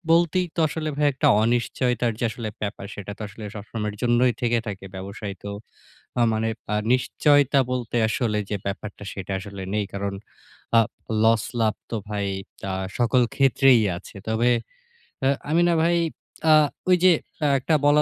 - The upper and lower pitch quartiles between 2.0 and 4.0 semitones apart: No, average, 4.4 semitones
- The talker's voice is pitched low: Yes, low, 115 Hz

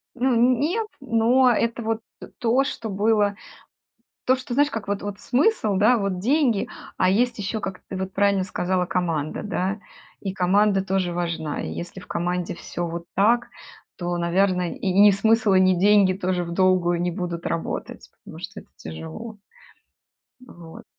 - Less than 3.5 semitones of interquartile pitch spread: No, average, 4.1 semitones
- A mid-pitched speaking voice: No, high, 195 Hz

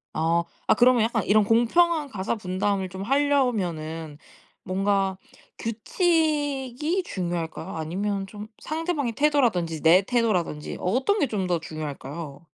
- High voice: Yes, high, 205 Hz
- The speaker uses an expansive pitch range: Yes, wide, 7.5 semitones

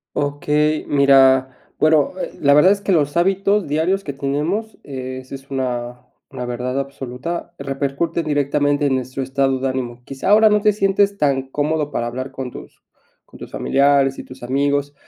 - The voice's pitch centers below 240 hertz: Yes, medium, 140 Hz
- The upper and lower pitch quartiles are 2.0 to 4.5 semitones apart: Yes, average, 3.0 semitones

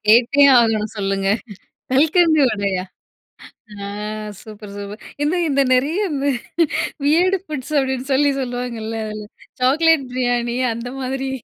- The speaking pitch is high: Yes, very high, 250 Hz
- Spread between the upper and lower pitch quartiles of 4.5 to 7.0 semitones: Yes, average, 4.8 semitones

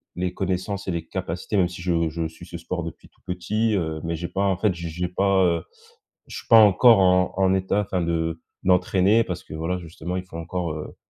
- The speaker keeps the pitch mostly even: Yes, narrow, 2.2 semitones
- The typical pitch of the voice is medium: No, very low, 90 Hz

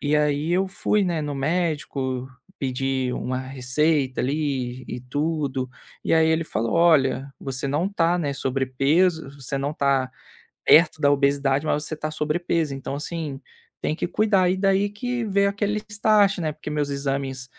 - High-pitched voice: No, medium, 145 Hz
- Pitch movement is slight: No, average, 3.7 semitones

